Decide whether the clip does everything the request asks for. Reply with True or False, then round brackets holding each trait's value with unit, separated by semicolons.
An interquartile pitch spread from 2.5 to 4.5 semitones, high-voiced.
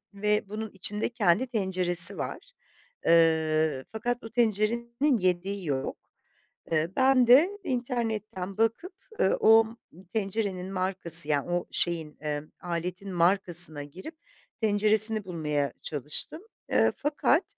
False (4.9 semitones; 195 Hz)